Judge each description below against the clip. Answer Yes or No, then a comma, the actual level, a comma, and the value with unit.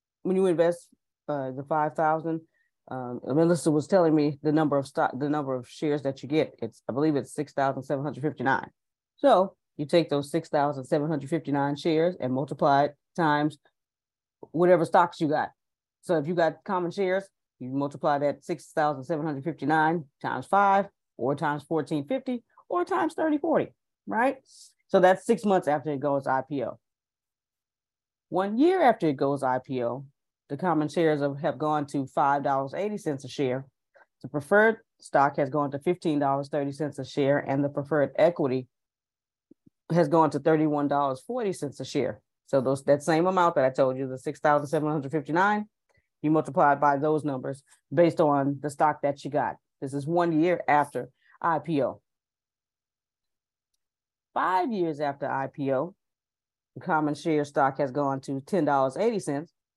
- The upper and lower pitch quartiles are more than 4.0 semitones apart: No, average, 3.2 semitones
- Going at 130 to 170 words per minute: Yes, average, 160 wpm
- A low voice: No, medium, 150 Hz